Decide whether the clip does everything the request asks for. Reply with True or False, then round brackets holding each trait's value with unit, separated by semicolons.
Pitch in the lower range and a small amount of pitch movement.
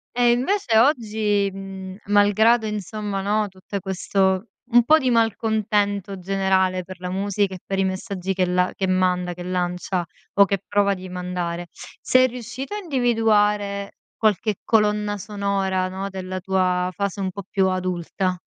False (195 Hz; 2.2 semitones)